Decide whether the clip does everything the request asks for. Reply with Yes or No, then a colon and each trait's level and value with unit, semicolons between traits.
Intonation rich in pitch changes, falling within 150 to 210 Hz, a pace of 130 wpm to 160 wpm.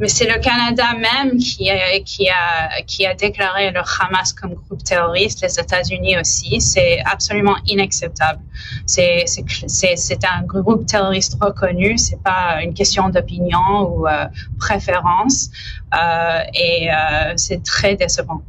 No: average, 2.9 semitones; high, 190 Hz; average, 150 wpm